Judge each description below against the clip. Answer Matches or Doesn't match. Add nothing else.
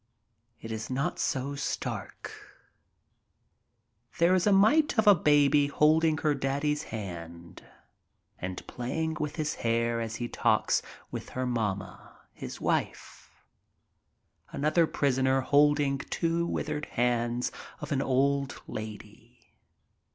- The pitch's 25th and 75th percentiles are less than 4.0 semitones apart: Doesn't match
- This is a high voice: Doesn't match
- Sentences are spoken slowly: Matches